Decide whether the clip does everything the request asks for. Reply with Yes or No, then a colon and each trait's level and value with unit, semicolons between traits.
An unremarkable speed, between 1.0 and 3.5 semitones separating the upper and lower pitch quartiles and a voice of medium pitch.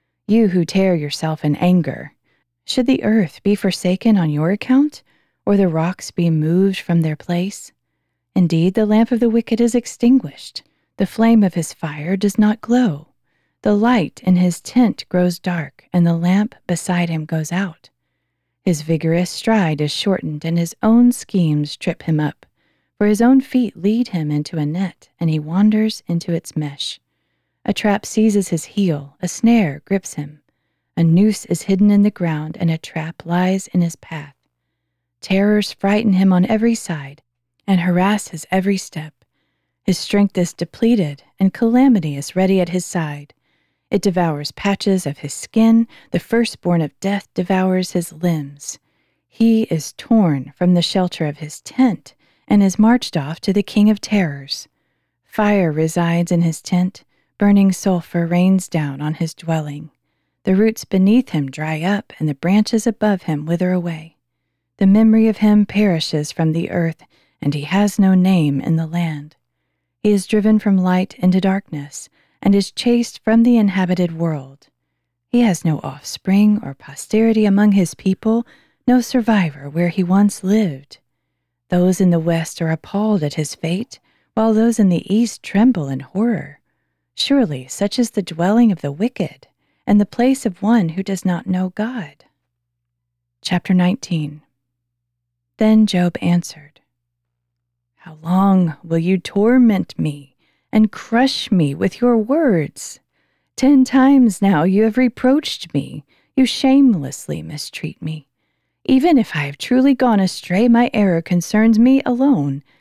No: average, 160 wpm; average, 5.2 semitones; medium, 180 Hz